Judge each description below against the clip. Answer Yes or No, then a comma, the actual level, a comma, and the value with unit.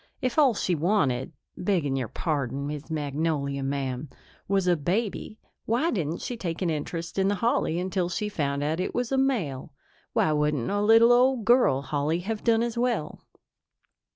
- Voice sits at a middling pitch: Yes, medium, 175 Hz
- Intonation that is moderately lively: No, wide, 7.3 semitones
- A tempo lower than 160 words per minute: No, average, 175 wpm